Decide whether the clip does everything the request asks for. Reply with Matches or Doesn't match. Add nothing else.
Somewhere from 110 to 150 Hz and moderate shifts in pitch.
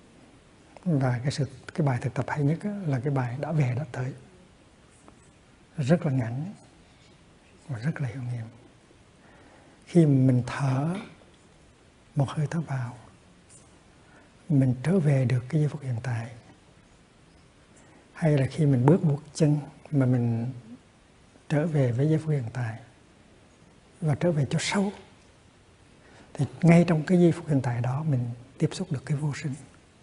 Matches